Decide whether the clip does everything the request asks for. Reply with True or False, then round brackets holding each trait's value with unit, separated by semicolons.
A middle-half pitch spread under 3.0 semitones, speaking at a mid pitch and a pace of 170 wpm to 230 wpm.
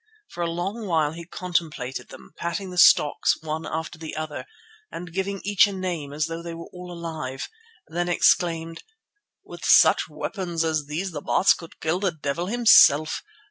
True (2.4 semitones; 170 Hz; 180 wpm)